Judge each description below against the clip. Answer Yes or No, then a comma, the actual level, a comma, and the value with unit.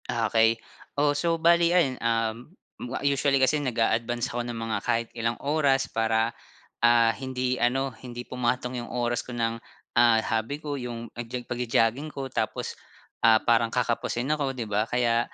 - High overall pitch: No, low, 120 Hz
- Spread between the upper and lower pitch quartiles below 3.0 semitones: Yes, narrow, 2.6 semitones